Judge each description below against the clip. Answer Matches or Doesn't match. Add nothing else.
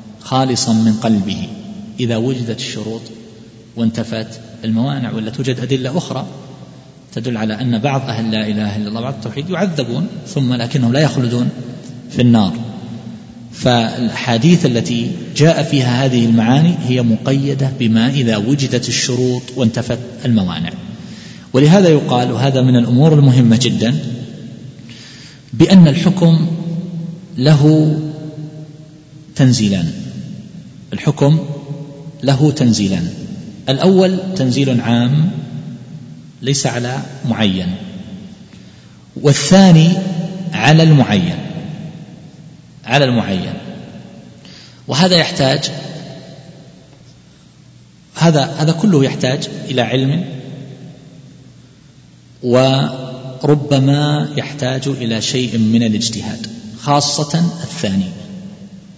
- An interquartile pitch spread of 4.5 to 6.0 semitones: Matches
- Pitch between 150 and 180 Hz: Doesn't match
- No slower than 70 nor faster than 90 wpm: Matches